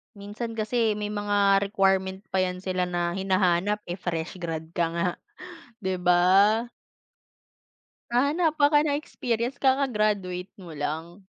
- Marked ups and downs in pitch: No, average, 3.3 semitones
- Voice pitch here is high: Yes, high, 195 Hz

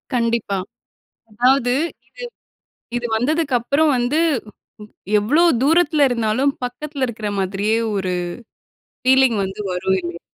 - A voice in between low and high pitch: No, high, 245 Hz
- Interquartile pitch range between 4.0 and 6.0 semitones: Yes, average, 5.0 semitones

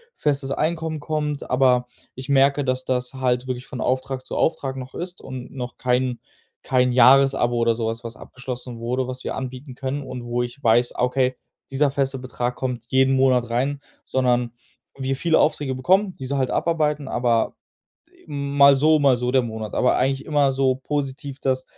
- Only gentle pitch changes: Yes, narrow, 2.0 semitones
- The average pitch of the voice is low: Yes, low, 130 Hz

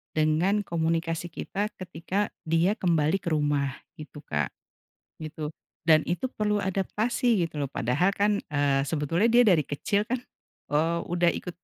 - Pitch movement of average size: Yes, average, 4.8 semitones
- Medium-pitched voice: Yes, medium, 170 Hz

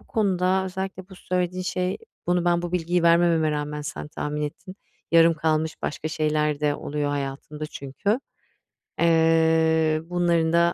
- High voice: No, medium, 165 Hz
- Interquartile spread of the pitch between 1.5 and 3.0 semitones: Yes, average, 2.7 semitones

